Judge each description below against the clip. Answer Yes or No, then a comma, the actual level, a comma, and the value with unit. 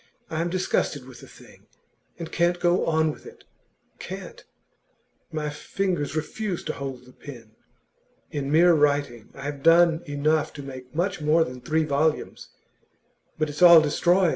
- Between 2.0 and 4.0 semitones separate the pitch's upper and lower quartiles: Yes, average, 3.2 semitones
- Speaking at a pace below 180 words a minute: Yes, average, 160 wpm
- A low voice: No, medium, 155 Hz